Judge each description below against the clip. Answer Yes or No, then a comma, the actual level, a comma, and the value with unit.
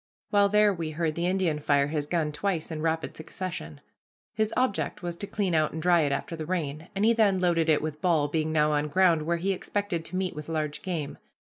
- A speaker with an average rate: No, fast, 230 wpm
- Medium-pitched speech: Yes, medium, 165 Hz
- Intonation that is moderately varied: Yes, average, 3.5 semitones